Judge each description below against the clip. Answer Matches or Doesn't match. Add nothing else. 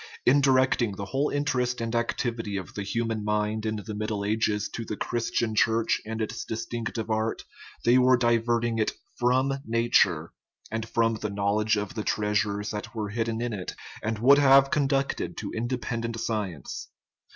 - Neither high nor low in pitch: Doesn't match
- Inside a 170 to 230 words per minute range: Matches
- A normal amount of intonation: Doesn't match